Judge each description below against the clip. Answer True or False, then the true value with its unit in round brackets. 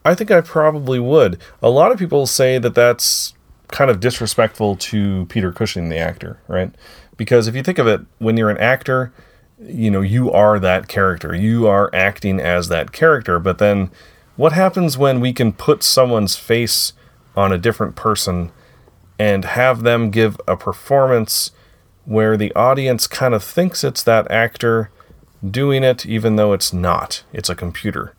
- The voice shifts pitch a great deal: False (4.5 semitones)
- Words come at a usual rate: True (170 wpm)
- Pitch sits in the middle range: False (110 Hz)